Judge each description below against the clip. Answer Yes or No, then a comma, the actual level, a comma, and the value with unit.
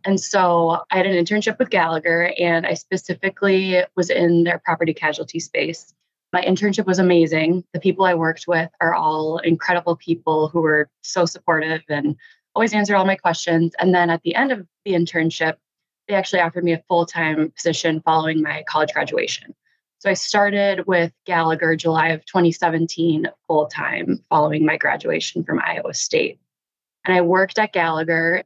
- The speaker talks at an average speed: Yes, average, 165 wpm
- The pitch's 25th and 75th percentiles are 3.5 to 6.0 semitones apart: No, narrow, 2.5 semitones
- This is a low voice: No, medium, 170 Hz